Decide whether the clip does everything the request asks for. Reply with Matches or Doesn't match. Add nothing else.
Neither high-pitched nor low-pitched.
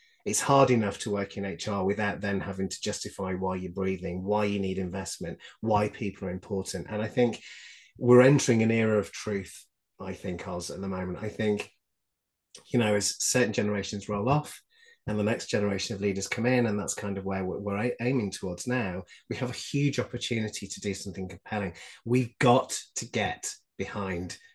Doesn't match